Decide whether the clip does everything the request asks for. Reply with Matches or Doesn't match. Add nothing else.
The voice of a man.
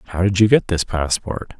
Matches